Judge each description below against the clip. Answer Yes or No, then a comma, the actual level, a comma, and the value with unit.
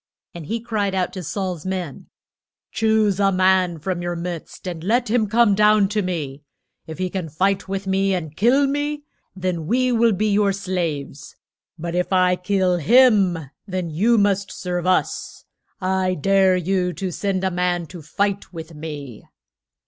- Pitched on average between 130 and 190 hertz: Yes, medium, 185 Hz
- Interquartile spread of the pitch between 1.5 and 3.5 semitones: Yes, average, 2.7 semitones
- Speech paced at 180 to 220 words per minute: No, average, 170 wpm